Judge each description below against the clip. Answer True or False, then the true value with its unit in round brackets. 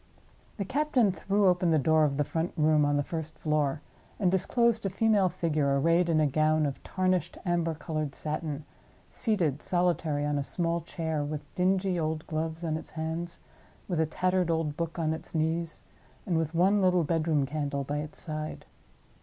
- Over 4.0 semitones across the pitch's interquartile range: False (2.8 semitones)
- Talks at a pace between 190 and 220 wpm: False (180 wpm)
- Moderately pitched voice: True (160 Hz)